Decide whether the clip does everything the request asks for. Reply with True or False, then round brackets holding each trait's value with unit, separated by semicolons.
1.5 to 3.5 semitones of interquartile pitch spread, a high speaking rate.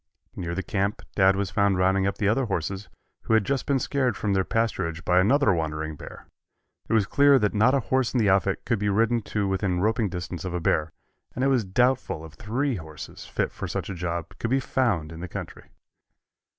False (4.6 semitones; 220 wpm)